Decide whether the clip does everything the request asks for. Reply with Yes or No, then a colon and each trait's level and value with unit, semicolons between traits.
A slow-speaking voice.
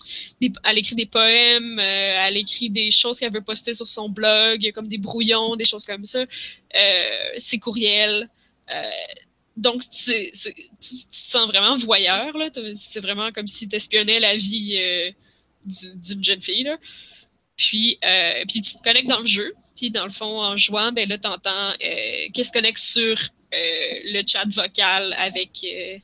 No: average, 185 wpm